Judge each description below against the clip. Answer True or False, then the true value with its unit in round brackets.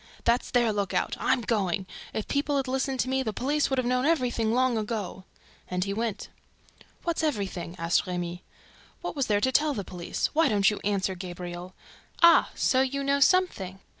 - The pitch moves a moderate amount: False (5.8 semitones)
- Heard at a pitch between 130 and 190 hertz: False (230 Hz)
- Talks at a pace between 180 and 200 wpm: True (185 wpm)